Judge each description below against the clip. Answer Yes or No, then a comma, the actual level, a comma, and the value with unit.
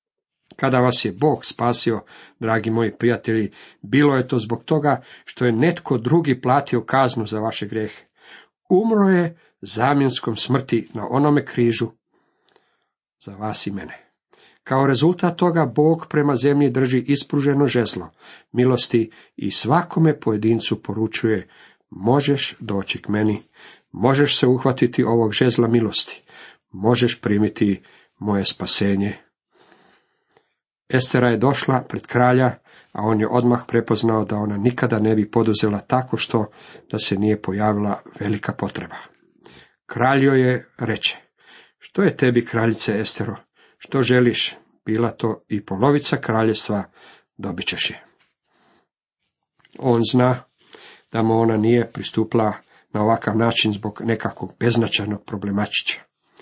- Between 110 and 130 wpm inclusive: Yes, average, 125 wpm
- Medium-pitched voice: No, low, 115 Hz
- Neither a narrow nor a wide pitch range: Yes, average, 3.4 semitones